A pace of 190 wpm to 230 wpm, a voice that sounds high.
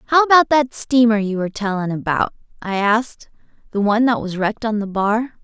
Yes: average, 200 wpm; high, 220 Hz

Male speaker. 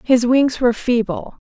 No: female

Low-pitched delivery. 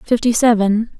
No: high, 225 Hz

